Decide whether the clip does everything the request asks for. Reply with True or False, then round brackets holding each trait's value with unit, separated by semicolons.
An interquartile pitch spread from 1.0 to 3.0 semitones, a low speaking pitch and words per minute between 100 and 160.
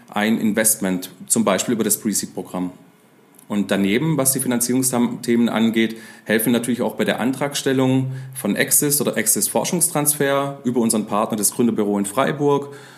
False (3.8 semitones; 120 Hz; 150 wpm)